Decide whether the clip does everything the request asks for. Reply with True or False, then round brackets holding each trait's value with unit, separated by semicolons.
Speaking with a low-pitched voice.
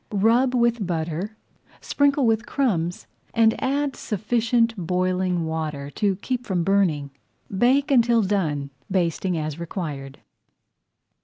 False (195 Hz)